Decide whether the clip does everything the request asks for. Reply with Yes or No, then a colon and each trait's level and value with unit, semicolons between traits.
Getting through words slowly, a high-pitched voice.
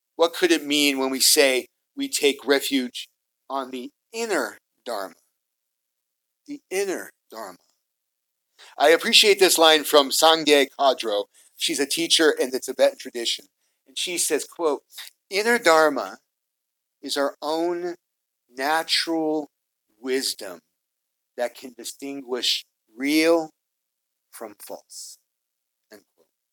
No: slow, 110 wpm; medium, 140 Hz